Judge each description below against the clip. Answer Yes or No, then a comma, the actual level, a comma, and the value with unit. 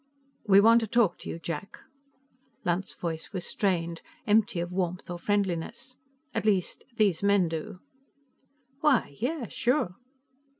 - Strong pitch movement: No, average, 4.3 semitones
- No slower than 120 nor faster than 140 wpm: Yes, slow, 135 wpm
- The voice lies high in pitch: Yes, high, 195 Hz